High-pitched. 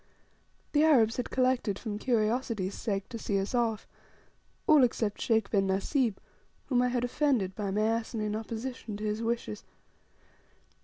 Yes: high, 225 Hz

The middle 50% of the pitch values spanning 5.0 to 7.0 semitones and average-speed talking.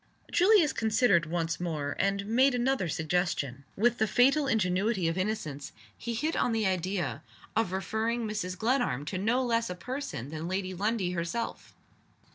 Yes: average, 5.3 semitones; average, 155 wpm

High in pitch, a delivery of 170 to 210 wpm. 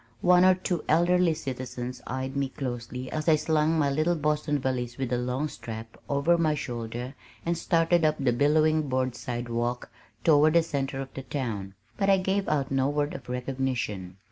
No: medium, 140 Hz; average, 180 wpm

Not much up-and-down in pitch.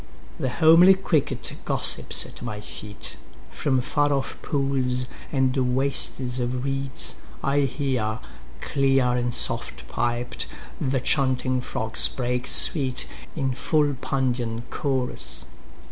Yes: narrow, 2.0 semitones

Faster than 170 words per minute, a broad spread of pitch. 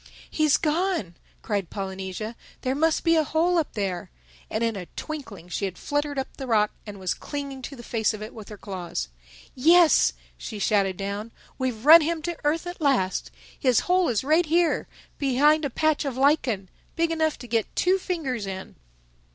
Yes: average, 185 wpm; wide, 7.1 semitones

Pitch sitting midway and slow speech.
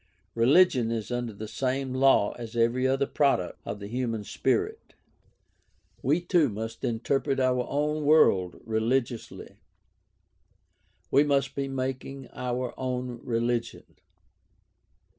No: low, 125 Hz; slow, 115 wpm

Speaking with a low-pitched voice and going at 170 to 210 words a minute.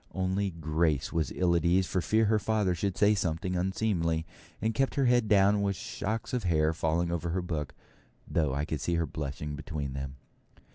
Yes: very low, 85 Hz; average, 195 wpm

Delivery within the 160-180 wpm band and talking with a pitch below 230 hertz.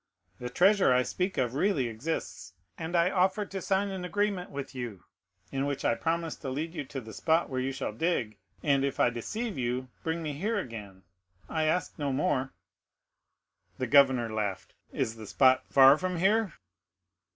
Yes: average, 175 wpm; medium, 140 Hz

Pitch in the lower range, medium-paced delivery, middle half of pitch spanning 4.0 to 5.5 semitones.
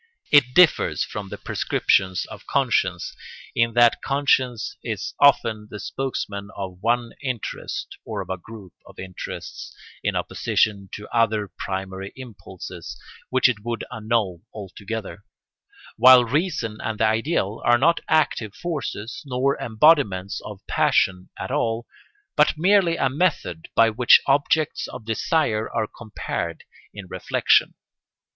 No: low, 115 Hz; slow, 130 wpm; average, 4.7 semitones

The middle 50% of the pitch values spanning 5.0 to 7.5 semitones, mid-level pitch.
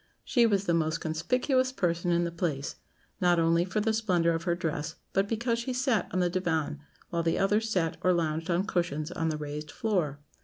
No: average, 4.1 semitones; medium, 175 Hz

